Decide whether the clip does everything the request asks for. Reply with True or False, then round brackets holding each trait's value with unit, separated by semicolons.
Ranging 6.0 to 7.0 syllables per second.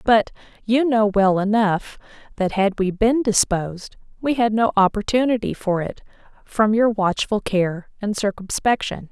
False (4.4 syllables/s)